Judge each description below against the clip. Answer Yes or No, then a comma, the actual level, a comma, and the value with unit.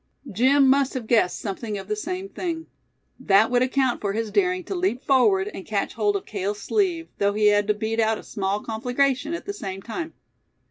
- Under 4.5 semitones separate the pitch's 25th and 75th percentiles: No, average, 5.3 semitones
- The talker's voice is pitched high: Yes, high, 225 Hz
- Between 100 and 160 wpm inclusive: No, fast, 205 wpm